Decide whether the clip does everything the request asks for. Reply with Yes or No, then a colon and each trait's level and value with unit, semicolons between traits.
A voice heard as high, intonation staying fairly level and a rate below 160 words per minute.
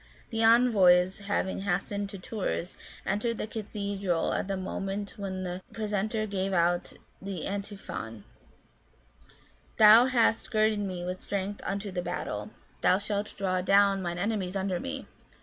Yes: high, 195 Hz; narrow, 2.2 semitones; average, 145 wpm